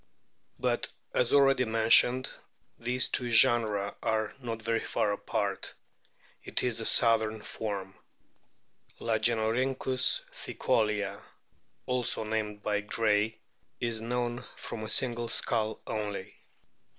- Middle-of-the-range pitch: No, low, 115 Hz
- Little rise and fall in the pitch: Yes, narrow, 2.0 semitones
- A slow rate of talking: Yes, slow, 105 wpm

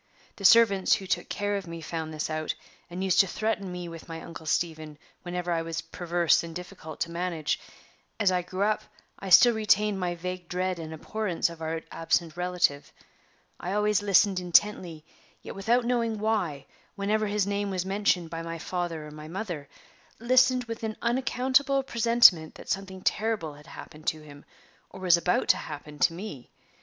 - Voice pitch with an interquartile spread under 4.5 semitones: Yes, average, 4.1 semitones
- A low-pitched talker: No, medium, 180 Hz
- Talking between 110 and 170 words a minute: No, average, 180 wpm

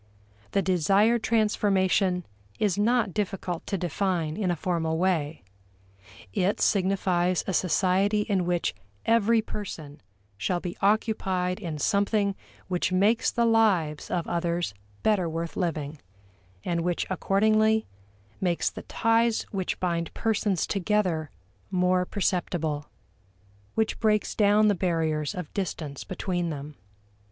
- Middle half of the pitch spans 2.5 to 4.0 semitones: Yes, average, 3.5 semitones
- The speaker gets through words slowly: Yes, slow, 120 wpm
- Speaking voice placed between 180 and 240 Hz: Yes, medium, 185 Hz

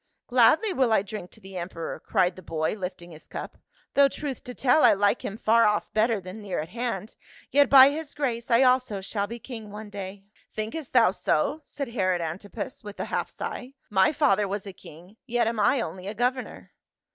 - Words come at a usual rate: No, fast, 215 wpm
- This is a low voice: No, high, 215 Hz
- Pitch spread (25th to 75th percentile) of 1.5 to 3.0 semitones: No, average, 4.6 semitones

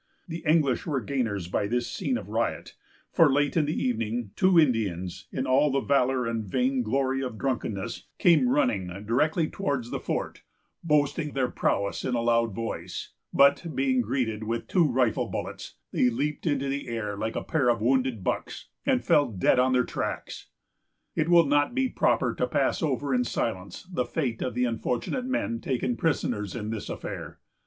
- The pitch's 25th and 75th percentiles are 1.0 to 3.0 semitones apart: No, average, 4.1 semitones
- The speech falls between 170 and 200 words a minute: Yes, average, 180 wpm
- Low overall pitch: Yes, low, 130 Hz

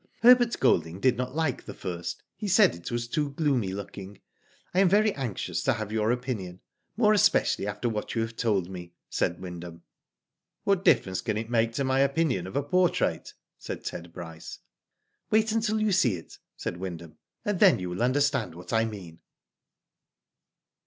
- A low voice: Yes, low, 115 Hz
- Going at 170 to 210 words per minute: Yes, average, 180 wpm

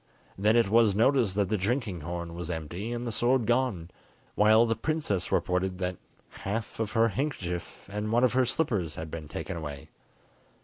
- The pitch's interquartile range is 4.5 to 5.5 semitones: Yes, average, 5.0 semitones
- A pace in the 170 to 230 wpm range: Yes, average, 180 wpm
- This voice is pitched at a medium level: No, low, 105 Hz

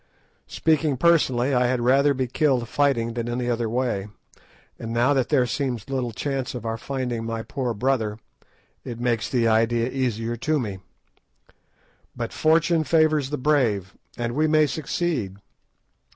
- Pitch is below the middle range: Yes, low, 125 Hz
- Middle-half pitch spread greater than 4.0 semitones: No, average, 3.4 semitones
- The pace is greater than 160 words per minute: No, average, 150 wpm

